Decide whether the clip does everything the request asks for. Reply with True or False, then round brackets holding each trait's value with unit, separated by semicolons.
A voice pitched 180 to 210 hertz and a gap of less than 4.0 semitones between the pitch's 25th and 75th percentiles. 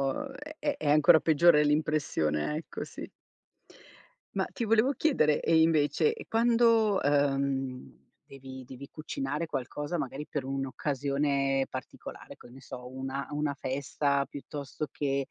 False (145 Hz; 2.6 semitones)